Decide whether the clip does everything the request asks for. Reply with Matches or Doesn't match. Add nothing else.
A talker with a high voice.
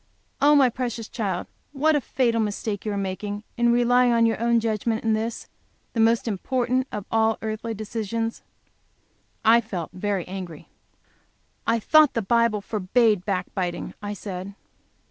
Matches